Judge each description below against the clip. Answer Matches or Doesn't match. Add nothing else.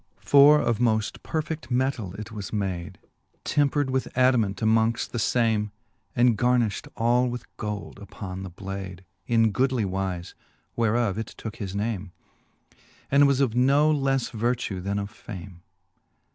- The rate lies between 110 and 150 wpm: Matches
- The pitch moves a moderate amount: Matches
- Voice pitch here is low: Matches